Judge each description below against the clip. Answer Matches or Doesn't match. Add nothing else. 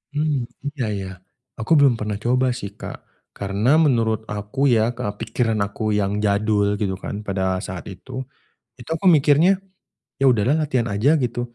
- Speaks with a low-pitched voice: Matches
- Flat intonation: Doesn't match